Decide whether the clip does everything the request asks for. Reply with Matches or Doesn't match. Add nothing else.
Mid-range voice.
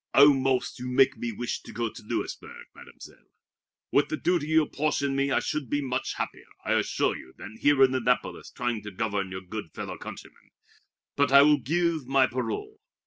Doesn't match